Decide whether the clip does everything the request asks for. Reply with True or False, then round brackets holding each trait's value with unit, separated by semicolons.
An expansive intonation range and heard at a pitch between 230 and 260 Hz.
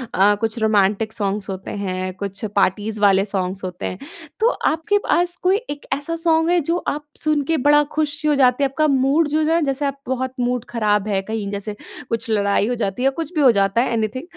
True (6.5 semitones; 245 Hz)